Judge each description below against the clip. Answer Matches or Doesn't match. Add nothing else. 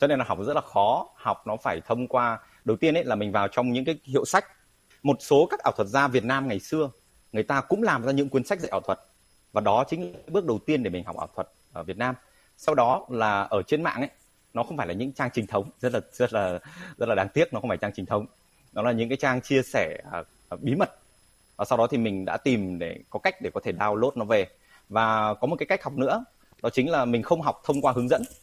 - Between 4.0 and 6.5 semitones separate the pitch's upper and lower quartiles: Matches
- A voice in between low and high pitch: Doesn't match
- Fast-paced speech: Matches